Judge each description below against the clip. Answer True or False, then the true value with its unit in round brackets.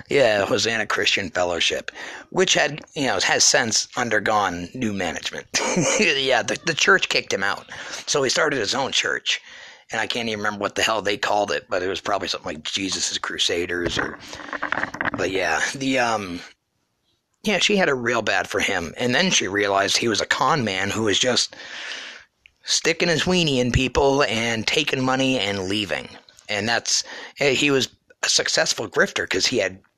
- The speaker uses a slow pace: False (180 wpm)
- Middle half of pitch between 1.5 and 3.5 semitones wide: False (5.1 semitones)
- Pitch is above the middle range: False (110 Hz)